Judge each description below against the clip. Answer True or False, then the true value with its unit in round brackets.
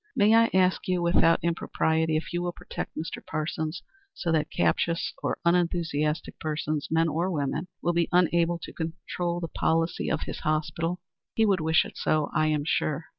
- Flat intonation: True (1.9 semitones)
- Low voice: False (165 Hz)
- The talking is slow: False (180 wpm)